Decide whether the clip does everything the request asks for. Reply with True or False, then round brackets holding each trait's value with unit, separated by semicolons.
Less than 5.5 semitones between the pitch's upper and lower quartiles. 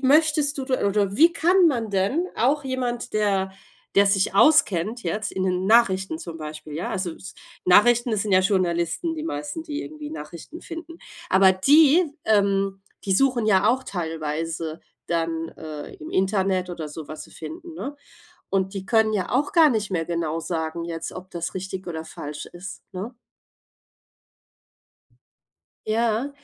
False (7.0 semitones)